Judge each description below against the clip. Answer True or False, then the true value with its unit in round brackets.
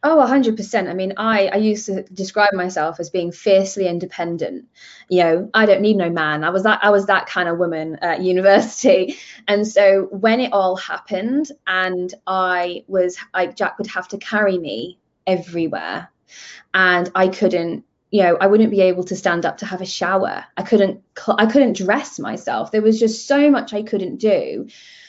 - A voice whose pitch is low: False (195 Hz)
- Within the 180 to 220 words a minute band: True (190 wpm)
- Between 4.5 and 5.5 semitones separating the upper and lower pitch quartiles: False (2.5 semitones)